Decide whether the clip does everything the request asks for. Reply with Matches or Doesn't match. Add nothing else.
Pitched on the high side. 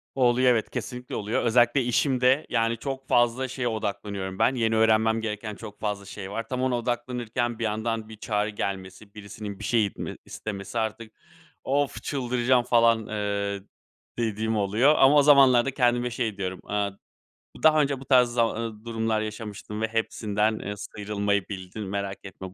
Doesn't match